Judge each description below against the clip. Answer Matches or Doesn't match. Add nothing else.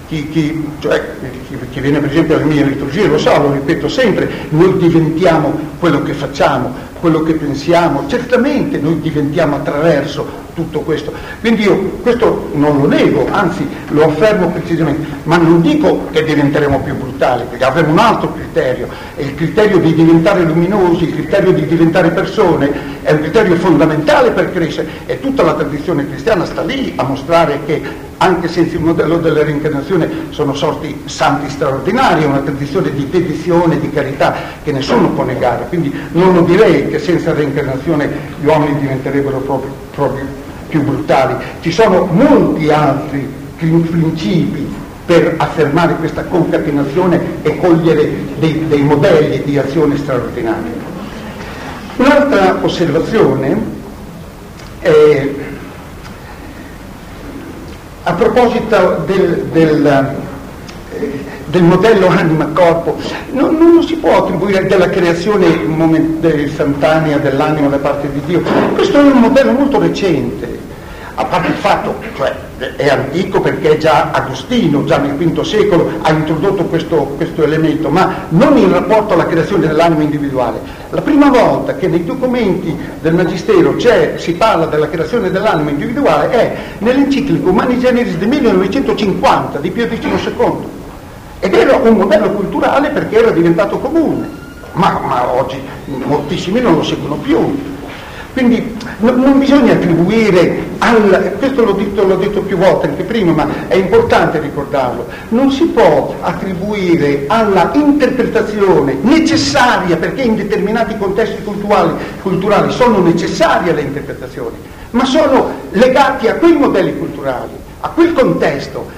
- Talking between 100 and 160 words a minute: Matches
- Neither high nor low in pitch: Matches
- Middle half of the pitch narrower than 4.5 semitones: Doesn't match